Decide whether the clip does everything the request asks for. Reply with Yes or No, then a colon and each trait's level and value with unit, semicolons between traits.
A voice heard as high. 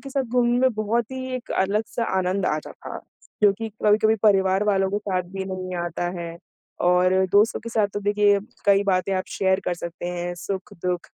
Yes: high, 200 Hz